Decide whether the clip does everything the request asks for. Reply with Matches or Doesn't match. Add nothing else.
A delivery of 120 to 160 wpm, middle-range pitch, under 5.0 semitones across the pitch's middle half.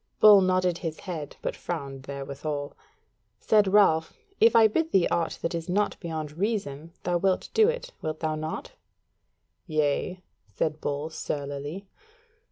Matches